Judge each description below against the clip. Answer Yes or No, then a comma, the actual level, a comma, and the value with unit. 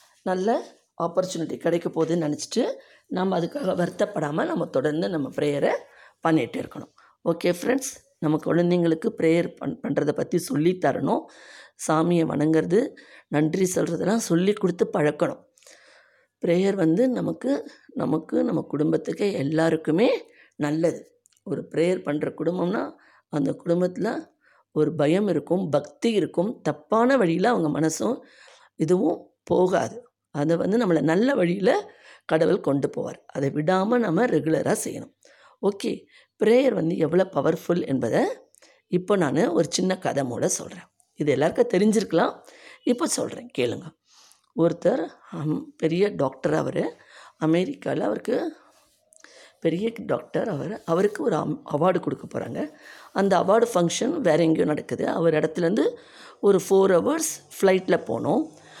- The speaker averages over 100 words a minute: Yes, average, 115 wpm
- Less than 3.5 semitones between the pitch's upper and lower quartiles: No, average, 4.6 semitones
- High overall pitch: No, medium, 175 Hz